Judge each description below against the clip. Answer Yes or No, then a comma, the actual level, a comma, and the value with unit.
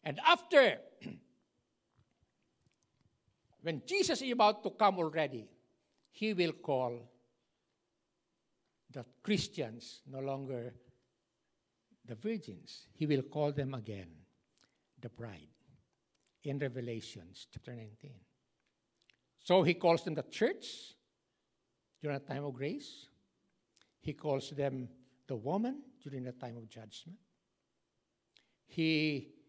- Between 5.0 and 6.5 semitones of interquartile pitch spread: Yes, wide, 5.6 semitones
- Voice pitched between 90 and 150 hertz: Yes, medium, 140 Hz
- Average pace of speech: No, slow, 105 wpm